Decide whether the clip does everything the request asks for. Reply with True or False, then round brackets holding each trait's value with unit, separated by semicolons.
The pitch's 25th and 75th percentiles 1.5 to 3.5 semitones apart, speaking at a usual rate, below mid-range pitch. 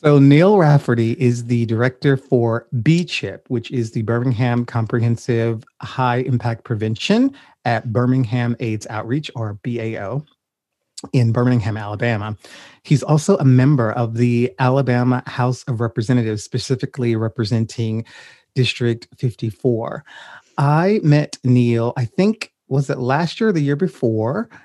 False (2.9 semitones; 125 wpm; 125 Hz)